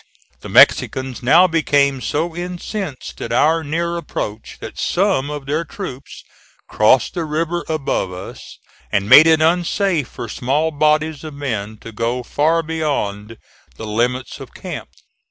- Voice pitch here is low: No, medium, 150 Hz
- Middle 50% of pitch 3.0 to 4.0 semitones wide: No, average, 4.8 semitones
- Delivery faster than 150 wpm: No, average, 145 wpm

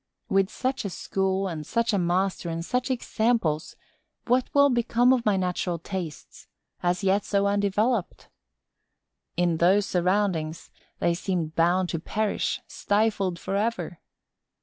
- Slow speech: Yes, slow, 130 wpm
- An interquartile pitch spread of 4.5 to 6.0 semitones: No, average, 3.8 semitones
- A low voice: No, high, 195 Hz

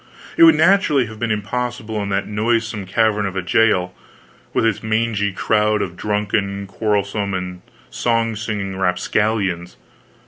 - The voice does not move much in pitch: Yes, narrow, 2.3 semitones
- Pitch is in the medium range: No, low, 105 Hz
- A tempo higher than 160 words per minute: No, average, 140 wpm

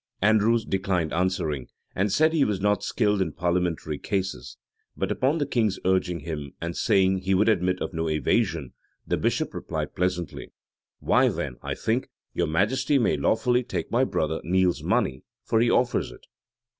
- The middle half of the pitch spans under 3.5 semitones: No, average, 4.8 semitones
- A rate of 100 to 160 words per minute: No, average, 170 wpm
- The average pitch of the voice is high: No, very low, 95 Hz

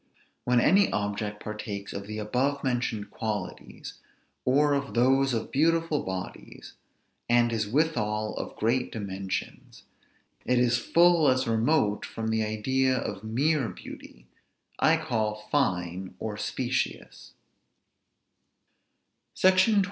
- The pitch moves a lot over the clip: No, average, 4.4 semitones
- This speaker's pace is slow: Yes, slow, 115 wpm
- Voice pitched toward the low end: Yes, low, 120 Hz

